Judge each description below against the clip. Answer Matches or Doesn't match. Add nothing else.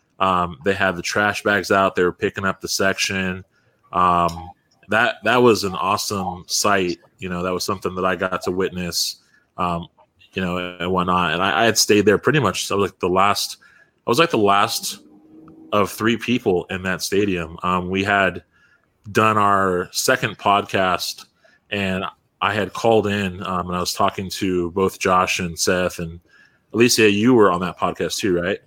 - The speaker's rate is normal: Matches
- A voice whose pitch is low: Matches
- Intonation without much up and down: Matches